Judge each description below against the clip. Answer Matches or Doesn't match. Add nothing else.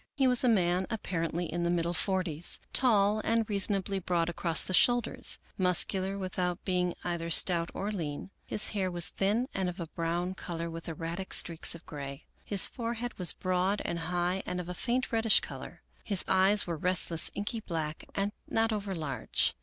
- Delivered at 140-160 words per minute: Doesn't match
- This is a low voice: Doesn't match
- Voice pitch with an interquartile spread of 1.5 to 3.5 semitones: Matches